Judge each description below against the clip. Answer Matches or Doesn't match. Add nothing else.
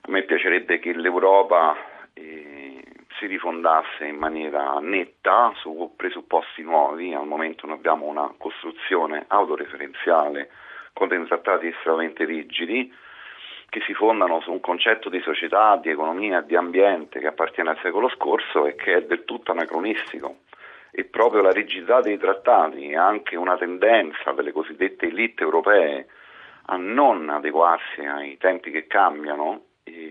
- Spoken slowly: Doesn't match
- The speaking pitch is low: Matches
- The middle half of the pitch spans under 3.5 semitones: Matches